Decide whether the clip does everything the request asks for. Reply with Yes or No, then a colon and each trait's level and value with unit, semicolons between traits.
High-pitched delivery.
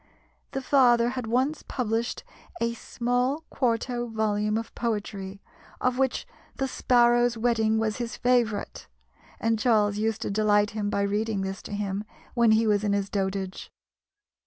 Yes: high, 225 Hz